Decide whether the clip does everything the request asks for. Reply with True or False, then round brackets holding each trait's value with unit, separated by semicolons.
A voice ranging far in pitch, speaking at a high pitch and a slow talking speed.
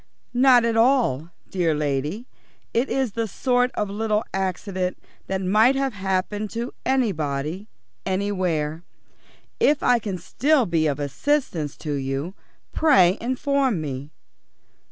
True (7.4 semitones; 195 Hz; 125 wpm)